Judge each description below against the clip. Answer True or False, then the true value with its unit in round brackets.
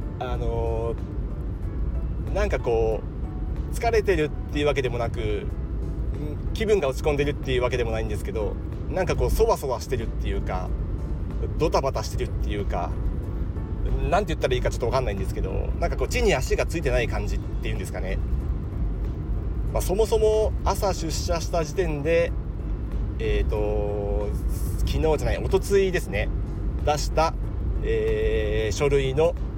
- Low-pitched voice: True (100 Hz)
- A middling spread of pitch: False (7.5 semitones)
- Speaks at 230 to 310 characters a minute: False (335 characters per minute)